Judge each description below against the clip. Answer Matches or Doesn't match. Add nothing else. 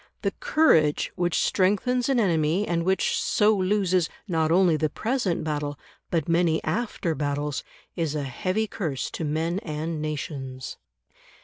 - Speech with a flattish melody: Doesn't match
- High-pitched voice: Doesn't match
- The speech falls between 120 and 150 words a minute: Matches